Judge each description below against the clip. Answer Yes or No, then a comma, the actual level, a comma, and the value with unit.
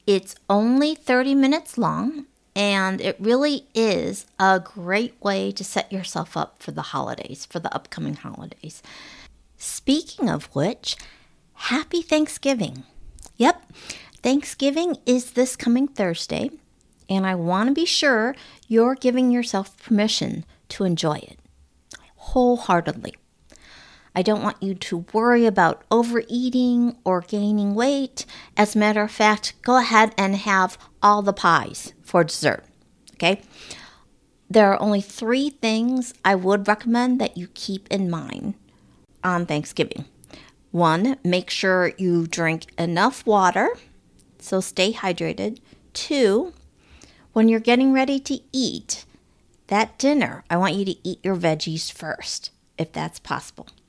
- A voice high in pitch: Yes, high, 215 Hz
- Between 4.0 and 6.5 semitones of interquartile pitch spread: Yes, average, 4.9 semitones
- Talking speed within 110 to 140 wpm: Yes, slow, 135 wpm